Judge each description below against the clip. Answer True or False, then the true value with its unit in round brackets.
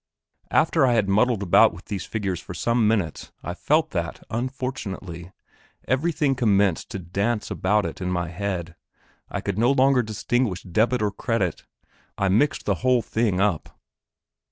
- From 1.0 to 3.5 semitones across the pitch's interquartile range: False (4.8 semitones)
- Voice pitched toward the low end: True (105 Hz)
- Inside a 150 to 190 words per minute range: True (155 wpm)